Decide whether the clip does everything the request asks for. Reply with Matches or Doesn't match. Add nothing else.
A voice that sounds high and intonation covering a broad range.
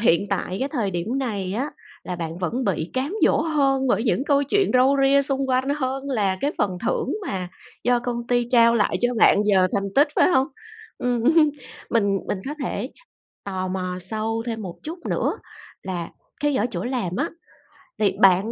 Matches